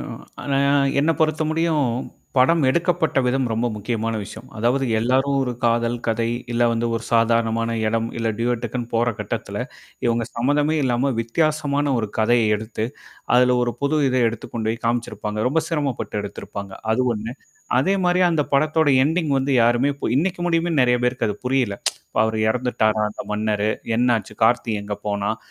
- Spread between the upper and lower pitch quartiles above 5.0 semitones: No, average, 3.9 semitones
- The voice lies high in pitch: No, low, 120 Hz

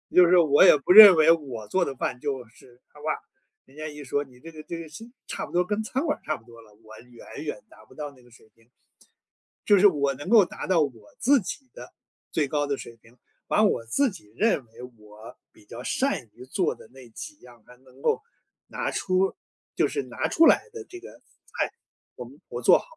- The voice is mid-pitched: Yes, medium, 145 Hz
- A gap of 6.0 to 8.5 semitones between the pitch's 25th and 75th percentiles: Yes, wide, 7.0 semitones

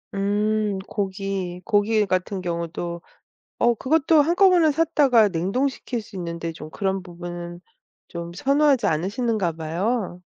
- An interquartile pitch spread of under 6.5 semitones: Yes, wide, 5.6 semitones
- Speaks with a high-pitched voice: Yes, high, 195 Hz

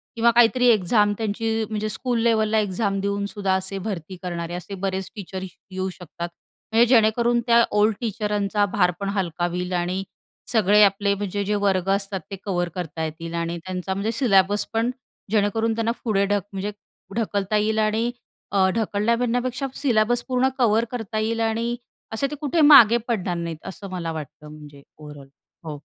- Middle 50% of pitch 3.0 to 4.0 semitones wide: Yes, average, 3.3 semitones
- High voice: Yes, high, 205 Hz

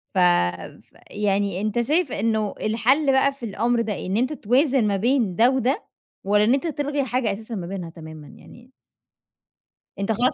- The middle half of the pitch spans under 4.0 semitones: No, average, 4.8 semitones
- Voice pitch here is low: No, high, 225 Hz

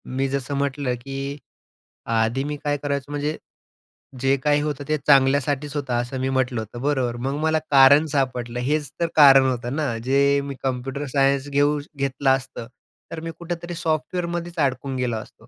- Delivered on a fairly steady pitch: Yes, narrow, 2.0 semitones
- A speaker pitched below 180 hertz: Yes, medium, 140 Hz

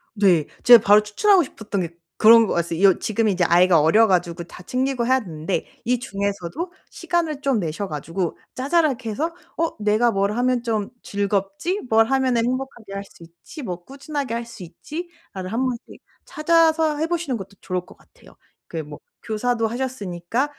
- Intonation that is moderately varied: No, wide, 6.0 semitones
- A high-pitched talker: Yes, high, 225 Hz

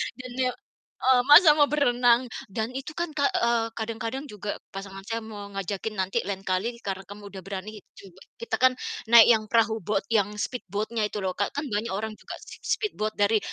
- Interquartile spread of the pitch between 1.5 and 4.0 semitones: Yes, average, 3.3 semitones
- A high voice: Yes, high, 220 Hz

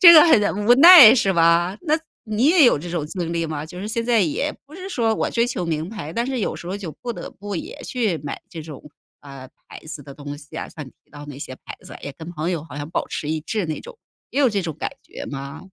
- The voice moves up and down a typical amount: No, wide, 7.2 semitones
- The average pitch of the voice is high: No, medium, 175 Hz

